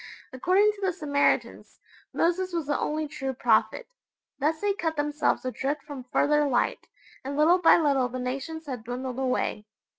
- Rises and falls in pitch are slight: No, average, 3.9 semitones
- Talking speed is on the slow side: No, average, 160 wpm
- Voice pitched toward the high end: Yes, very high, 290 Hz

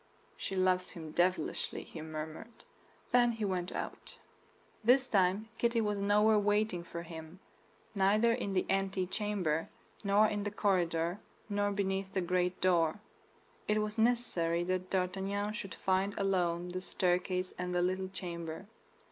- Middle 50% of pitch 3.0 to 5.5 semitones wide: No, narrow, 2.6 semitones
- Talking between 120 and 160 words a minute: Yes, average, 140 wpm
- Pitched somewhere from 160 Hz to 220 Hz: Yes, high, 190 Hz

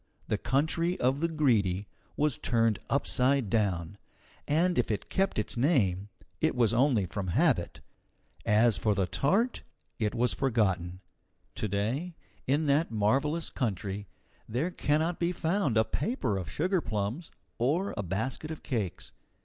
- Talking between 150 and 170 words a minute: No, average, 140 wpm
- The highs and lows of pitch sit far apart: Yes, wide, 7.1 semitones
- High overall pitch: No, low, 125 Hz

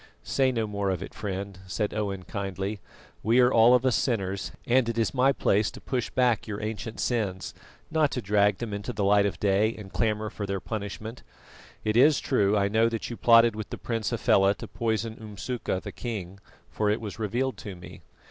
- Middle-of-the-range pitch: No, low, 110 Hz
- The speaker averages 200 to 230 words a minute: Yes, fast, 205 wpm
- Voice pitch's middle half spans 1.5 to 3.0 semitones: Yes, average, 2.7 semitones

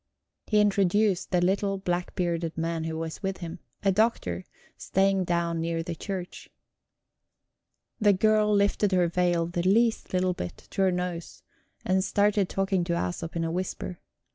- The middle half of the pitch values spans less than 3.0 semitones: Yes, narrow, 2.6 semitones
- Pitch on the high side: No, medium, 180 Hz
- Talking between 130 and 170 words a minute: Yes, average, 160 wpm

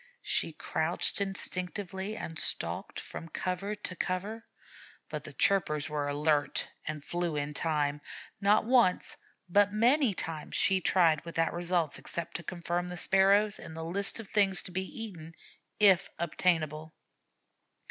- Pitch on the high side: No, medium, 180 Hz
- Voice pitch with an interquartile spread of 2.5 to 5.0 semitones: Yes, average, 3.7 semitones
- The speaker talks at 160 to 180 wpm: No, average, 140 wpm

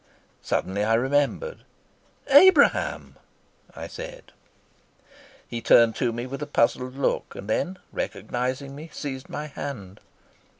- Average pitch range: Yes, average, 4.2 semitones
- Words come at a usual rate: No, slow, 120 wpm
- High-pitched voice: No, low, 135 Hz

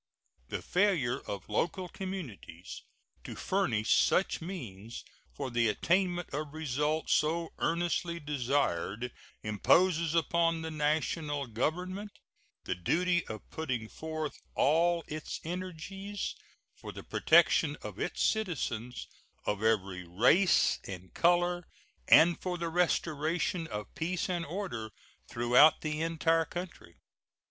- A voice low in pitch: No, medium, 160 Hz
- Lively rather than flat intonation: Yes, wide, 6.3 semitones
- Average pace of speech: No, slow, 115 wpm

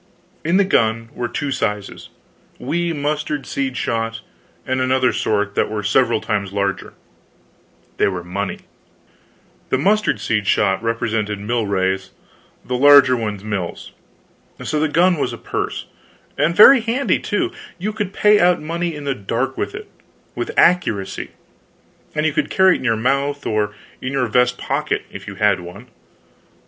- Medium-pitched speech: No, low, 125 Hz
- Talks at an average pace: Yes, average, 155 wpm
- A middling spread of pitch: No, wide, 6.6 semitones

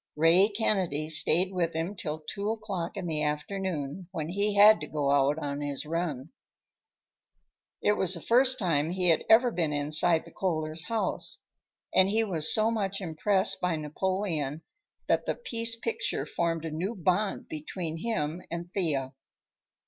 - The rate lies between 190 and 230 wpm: No, average, 160 wpm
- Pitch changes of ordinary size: Yes, average, 4.5 semitones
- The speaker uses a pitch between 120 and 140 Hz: No, medium, 175 Hz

